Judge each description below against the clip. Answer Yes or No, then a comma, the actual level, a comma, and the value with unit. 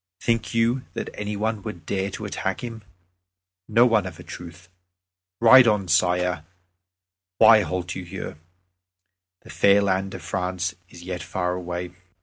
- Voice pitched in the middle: No, very low, 95 Hz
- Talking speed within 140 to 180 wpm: Yes, average, 150 wpm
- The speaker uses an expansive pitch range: No, average, 3.5 semitones